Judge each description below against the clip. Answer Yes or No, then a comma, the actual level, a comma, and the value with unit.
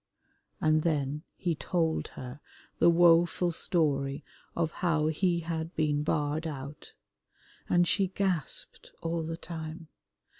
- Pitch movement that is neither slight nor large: No, narrow, 2.1 semitones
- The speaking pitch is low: No, medium, 160 Hz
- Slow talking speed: Yes, slow, 120 wpm